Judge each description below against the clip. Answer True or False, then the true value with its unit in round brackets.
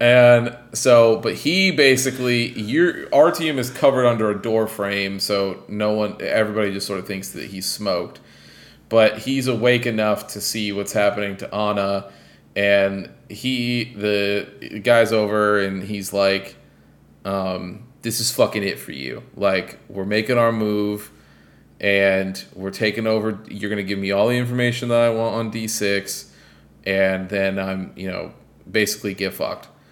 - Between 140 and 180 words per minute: True (160 wpm)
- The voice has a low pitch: True (105 Hz)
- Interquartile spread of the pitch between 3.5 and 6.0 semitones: False (2.8 semitones)